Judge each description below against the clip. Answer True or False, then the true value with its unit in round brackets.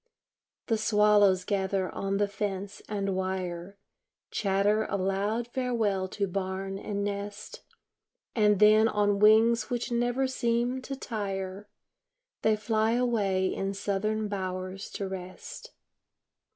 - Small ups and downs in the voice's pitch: True (2.2 semitones)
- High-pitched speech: True (205 Hz)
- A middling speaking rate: False (120 wpm)